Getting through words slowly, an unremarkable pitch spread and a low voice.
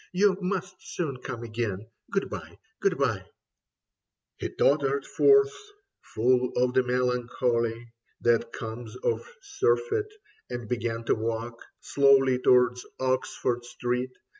Yes: slow, 115 wpm; average, 3.0 semitones; low, 125 Hz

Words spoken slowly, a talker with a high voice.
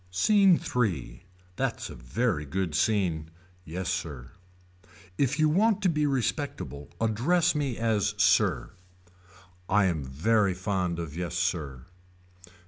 No: slow, 125 wpm; very low, 95 Hz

